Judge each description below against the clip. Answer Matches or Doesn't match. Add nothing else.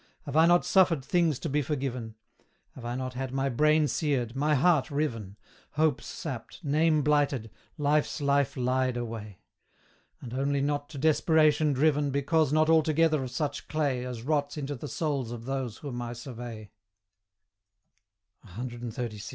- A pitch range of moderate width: Matches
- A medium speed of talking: Matches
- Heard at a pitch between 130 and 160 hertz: Matches